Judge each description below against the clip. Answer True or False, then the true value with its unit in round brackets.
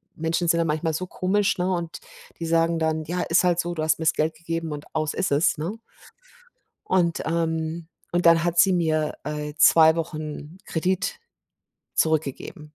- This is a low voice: False (165 Hz)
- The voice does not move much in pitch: True (1.7 semitones)